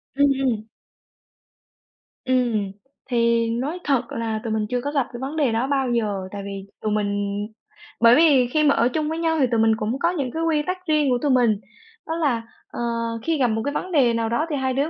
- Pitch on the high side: Yes, very high, 250 Hz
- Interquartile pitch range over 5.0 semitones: No, average, 4.4 semitones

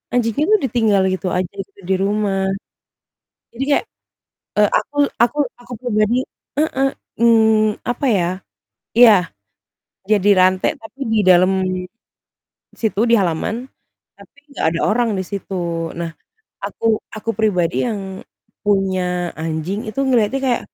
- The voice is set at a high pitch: Yes, high, 210 Hz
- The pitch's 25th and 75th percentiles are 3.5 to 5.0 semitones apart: Yes, average, 3.8 semitones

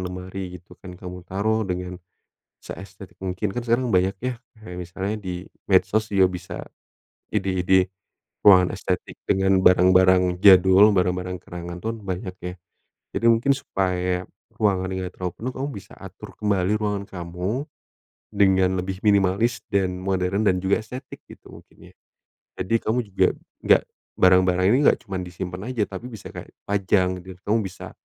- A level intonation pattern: Yes, narrow, 2.1 semitones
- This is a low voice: Yes, very low, 95 Hz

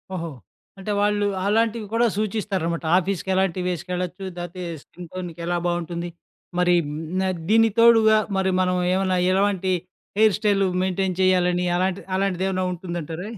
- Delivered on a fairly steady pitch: Yes, narrow, 2.3 semitones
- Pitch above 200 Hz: No, medium, 185 Hz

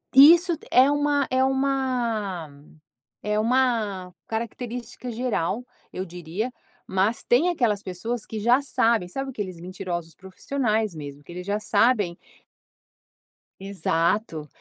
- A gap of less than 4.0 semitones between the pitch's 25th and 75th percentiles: No, wide, 5.6 semitones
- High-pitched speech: Yes, high, 220 Hz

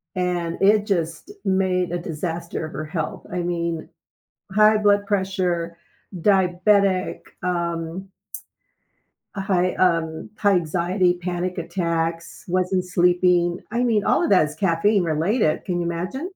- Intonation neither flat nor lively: No, narrow, 2.3 semitones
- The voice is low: No, medium, 180 Hz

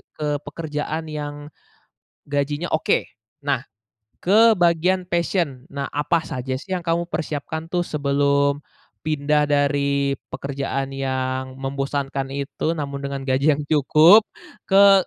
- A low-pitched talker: No, medium, 145 Hz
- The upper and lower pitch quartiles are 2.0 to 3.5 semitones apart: Yes, average, 2.9 semitones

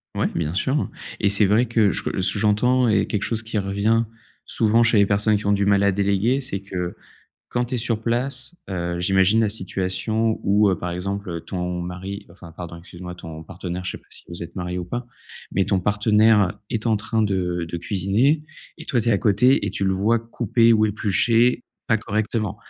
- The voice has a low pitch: Yes, low, 100 Hz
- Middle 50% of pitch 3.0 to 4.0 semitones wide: Yes, average, 3.5 semitones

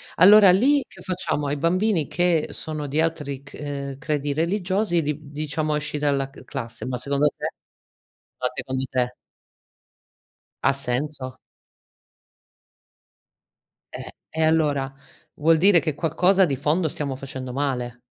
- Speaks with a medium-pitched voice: Yes, medium, 150 Hz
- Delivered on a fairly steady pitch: No, average, 3.4 semitones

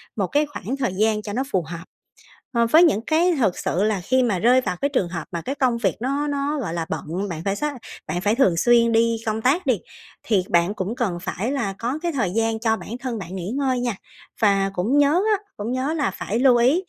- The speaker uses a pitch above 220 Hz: Yes, high, 230 Hz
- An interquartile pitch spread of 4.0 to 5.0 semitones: No, wide, 5.4 semitones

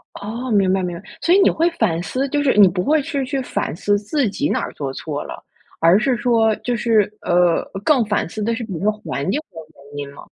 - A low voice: No, high, 215 Hz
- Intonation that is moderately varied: No, wide, 6.5 semitones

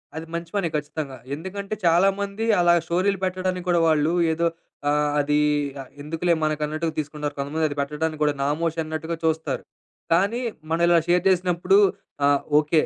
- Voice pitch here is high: No, medium, 165 Hz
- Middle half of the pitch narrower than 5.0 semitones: Yes, average, 2.9 semitones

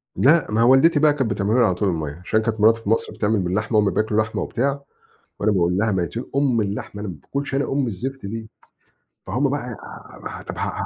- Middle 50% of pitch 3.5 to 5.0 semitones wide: Yes, average, 4.5 semitones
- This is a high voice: No, low, 110 Hz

